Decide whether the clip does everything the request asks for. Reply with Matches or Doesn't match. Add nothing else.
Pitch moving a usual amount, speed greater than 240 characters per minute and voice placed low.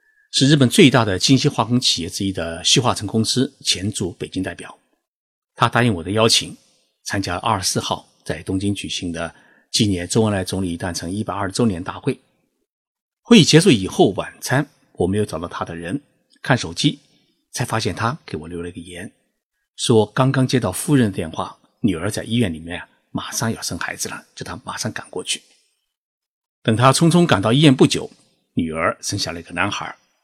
Doesn't match